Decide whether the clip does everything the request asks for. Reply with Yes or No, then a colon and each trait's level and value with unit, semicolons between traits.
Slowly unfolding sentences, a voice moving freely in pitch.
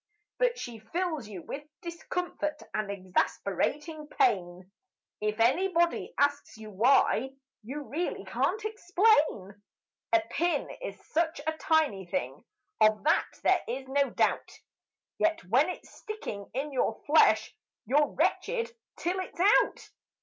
Yes: slow, 130 wpm; wide, 8.1 semitones